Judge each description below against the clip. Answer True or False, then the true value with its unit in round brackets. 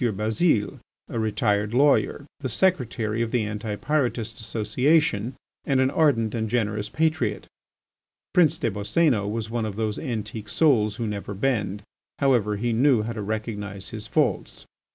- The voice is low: True (110 Hz)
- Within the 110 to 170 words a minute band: True (150 wpm)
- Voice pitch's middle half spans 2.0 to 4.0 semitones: True (3.6 semitones)